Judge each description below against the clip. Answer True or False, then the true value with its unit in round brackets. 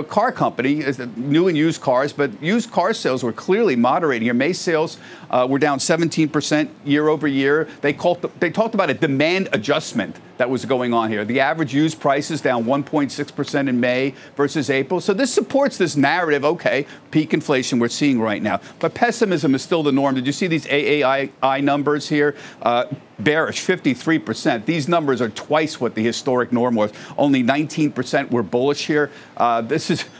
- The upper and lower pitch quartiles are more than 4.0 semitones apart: False (3.3 semitones)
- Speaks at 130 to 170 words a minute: False (185 wpm)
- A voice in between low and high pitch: True (145 Hz)